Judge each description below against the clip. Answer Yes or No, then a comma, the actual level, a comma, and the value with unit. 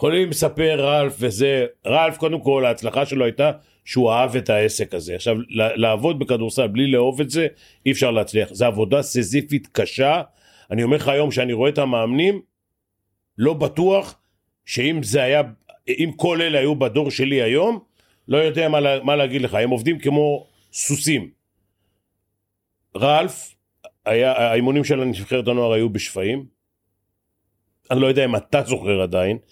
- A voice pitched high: No, low, 130 Hz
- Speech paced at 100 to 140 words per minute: No, fast, 150 wpm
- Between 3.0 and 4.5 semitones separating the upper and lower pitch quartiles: No, average, 5.2 semitones